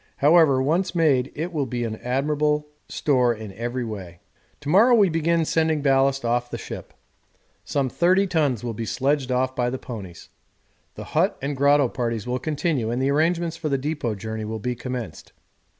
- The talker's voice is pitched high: No, low, 135 Hz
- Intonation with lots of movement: No, average, 4.3 semitones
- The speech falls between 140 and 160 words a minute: No, average, 180 wpm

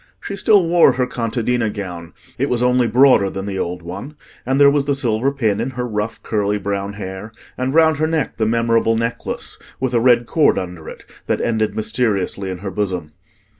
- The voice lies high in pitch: No, low, 115 Hz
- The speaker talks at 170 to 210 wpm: Yes, average, 200 wpm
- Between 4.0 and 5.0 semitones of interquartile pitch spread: Yes, average, 4.3 semitones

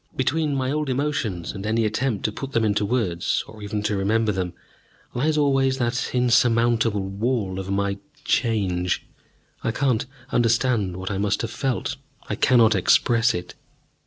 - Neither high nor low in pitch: No, low, 115 Hz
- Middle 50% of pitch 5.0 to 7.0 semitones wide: No, average, 4.2 semitones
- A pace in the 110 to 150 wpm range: No, average, 160 wpm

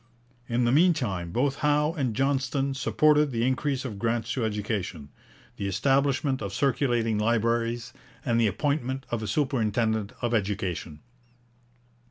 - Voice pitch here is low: Yes, low, 120 Hz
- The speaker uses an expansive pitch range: No, average, 4.1 semitones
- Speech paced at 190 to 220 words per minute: No, average, 140 wpm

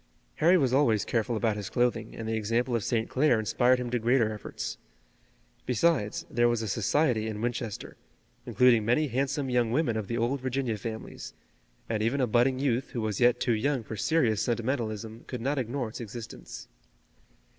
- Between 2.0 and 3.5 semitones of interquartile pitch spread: Yes, narrow, 2.6 semitones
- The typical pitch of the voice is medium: No, low, 120 Hz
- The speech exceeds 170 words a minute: Yes, average, 180 wpm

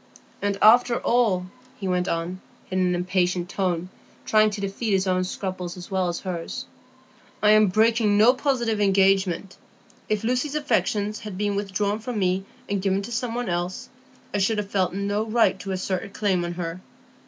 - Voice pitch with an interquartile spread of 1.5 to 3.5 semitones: Yes, average, 2.8 semitones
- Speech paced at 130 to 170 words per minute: No, average, 180 wpm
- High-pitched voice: Yes, high, 195 Hz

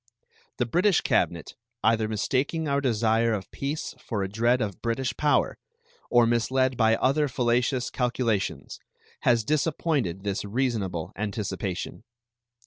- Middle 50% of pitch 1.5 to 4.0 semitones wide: Yes, average, 3.7 semitones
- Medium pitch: No, low, 120 Hz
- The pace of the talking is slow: Yes, slow, 125 wpm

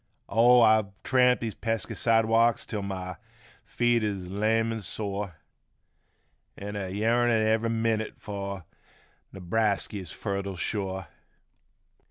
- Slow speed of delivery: Yes, slow, 110 wpm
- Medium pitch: No, low, 110 Hz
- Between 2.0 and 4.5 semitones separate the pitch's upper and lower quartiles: Yes, narrow, 2.5 semitones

